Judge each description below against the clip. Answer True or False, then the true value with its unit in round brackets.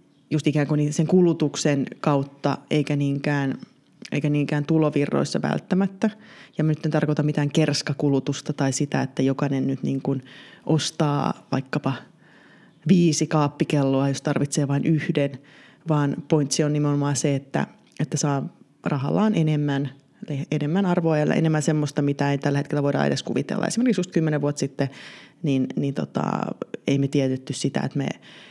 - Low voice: False (150 Hz)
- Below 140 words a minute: False (150 wpm)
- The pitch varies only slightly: True (2.1 semitones)